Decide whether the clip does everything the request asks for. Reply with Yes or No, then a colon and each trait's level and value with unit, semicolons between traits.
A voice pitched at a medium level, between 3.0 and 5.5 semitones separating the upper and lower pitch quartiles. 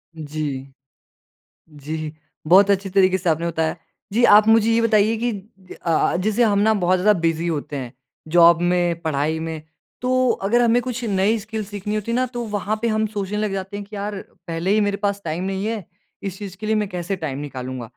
No: high, 195 Hz; average, 4.4 semitones